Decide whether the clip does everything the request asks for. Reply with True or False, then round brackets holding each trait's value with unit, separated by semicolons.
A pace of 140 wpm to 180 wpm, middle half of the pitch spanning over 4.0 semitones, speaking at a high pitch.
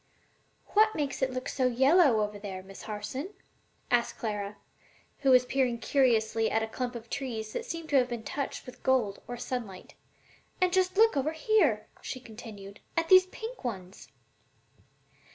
True (165 wpm; 5.1 semitones; 250 Hz)